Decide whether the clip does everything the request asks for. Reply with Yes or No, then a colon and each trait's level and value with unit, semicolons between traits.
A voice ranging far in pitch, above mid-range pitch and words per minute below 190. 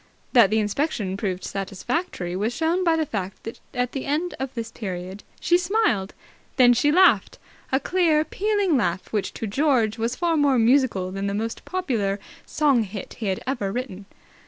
Yes: wide, 7.4 semitones; high, 240 Hz; average, 180 wpm